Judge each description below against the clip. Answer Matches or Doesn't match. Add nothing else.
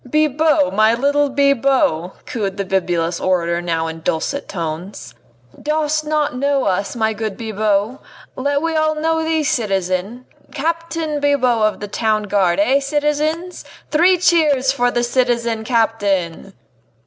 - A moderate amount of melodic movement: Doesn't match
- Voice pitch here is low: Doesn't match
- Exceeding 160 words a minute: Doesn't match